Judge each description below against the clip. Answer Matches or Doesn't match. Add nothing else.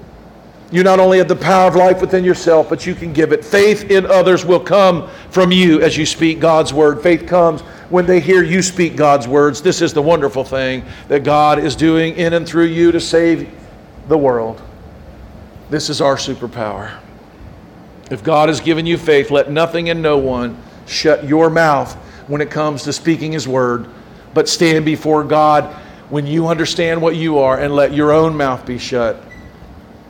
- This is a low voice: Doesn't match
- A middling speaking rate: Matches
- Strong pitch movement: Doesn't match